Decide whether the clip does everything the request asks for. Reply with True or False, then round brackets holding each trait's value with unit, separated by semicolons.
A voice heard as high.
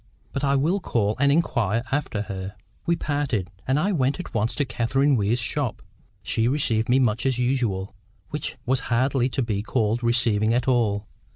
False (120 Hz)